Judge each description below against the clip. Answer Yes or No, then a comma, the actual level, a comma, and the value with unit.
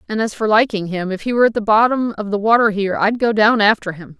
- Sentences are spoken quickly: Yes, fast, 285 wpm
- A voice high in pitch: Yes, high, 215 Hz